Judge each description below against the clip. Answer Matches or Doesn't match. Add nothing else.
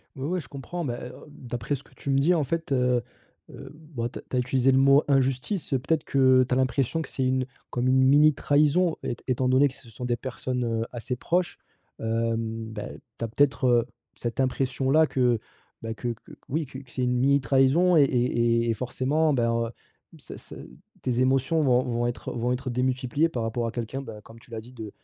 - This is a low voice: Matches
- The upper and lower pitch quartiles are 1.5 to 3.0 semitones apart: Matches